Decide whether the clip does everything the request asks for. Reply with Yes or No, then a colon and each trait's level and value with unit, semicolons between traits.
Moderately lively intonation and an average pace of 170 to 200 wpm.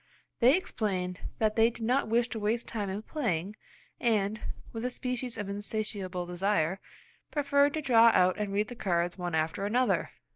Yes: average, 4.1 semitones; average, 175 wpm